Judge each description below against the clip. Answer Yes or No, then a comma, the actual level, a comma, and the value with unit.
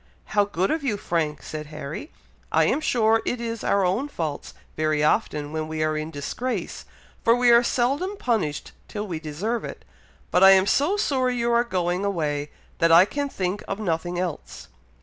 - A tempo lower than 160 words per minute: No, average, 190 wpm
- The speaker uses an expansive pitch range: Yes, wide, 7.1 semitones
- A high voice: Yes, high, 195 Hz